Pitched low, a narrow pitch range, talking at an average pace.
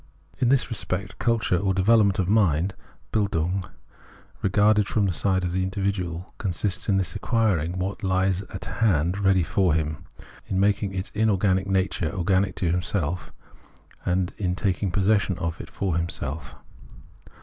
Yes: very low, 95 Hz; narrow, 2.2 semitones; average, 150 wpm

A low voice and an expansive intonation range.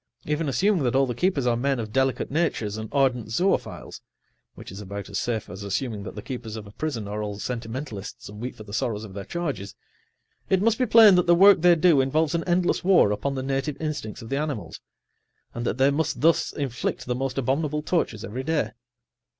Yes: low, 130 Hz; wide, 6.4 semitones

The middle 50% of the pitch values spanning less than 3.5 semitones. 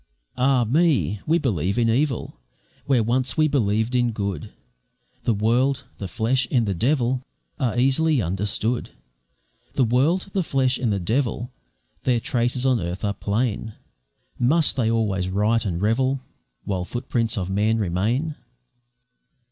No: average, 4.0 semitones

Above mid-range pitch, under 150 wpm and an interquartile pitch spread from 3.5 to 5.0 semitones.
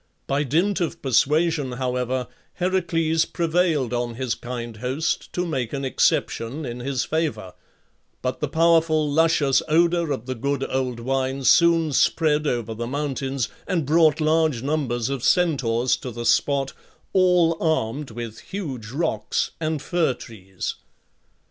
No: medium, 140 Hz; average, 140 wpm; average, 4.6 semitones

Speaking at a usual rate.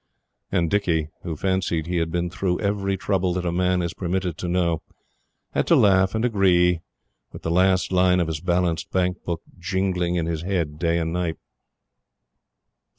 Yes: average, 175 wpm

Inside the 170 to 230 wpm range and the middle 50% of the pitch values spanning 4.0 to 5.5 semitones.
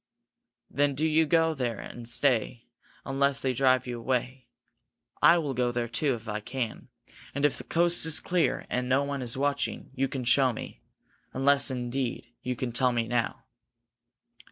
No: average, 175 wpm; average, 2.7 semitones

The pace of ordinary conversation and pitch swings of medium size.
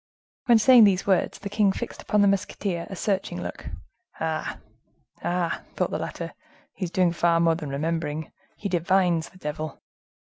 Yes: average, 170 wpm; average, 3.4 semitones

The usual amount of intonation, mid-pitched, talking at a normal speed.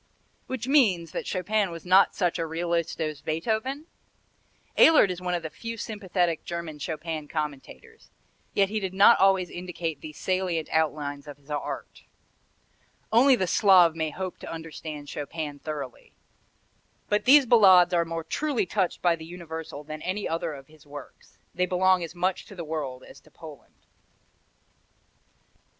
Yes: average, 3.5 semitones; medium, 170 Hz; average, 160 wpm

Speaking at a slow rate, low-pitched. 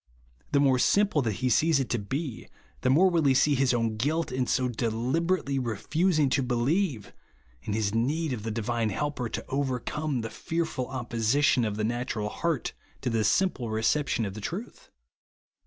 No: average, 185 wpm; low, 130 Hz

